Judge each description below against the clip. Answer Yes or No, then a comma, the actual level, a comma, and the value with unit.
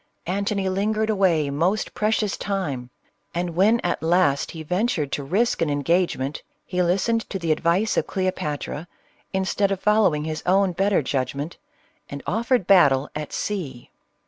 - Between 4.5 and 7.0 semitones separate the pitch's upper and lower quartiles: Yes, average, 4.8 semitones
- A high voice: No, medium, 180 Hz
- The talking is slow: No, average, 145 wpm